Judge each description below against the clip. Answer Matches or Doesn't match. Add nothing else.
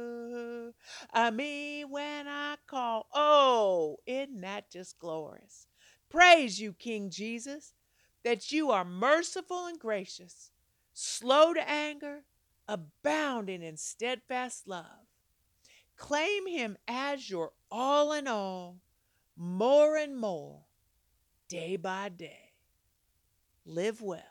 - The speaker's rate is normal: Doesn't match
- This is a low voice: Doesn't match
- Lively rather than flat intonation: Matches